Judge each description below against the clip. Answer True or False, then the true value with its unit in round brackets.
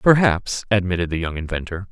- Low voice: True (95 Hz)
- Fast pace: False (155 wpm)